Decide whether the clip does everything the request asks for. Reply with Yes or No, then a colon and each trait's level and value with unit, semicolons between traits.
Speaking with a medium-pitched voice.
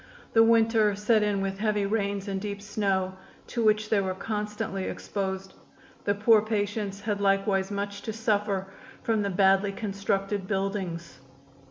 No: high, 200 Hz